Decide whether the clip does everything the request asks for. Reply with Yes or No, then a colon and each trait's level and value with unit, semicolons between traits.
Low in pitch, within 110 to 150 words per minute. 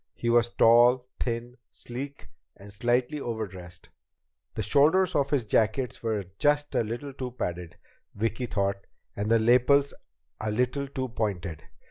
Yes: low, 120 Hz; average, 140 wpm